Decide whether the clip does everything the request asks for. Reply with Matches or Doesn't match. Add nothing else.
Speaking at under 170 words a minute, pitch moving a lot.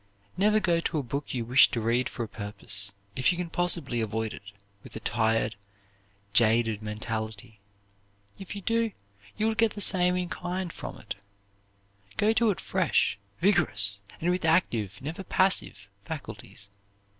Matches